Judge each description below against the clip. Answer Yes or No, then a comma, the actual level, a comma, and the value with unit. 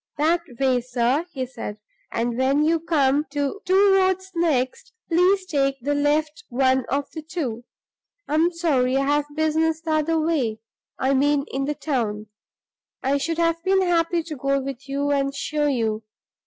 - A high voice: Yes, very high, 290 Hz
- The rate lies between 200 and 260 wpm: No, average, 170 wpm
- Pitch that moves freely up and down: No, average, 3.7 semitones